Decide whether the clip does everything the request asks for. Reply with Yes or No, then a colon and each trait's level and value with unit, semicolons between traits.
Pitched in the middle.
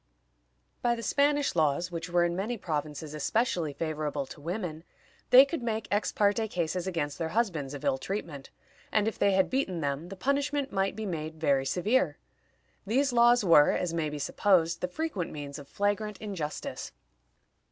Yes: medium, 180 Hz